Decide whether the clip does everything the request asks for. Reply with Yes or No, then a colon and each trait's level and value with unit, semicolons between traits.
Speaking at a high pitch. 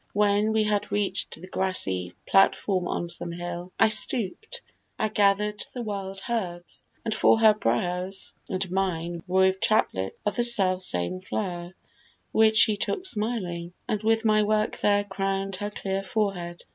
Yes: high, 195 Hz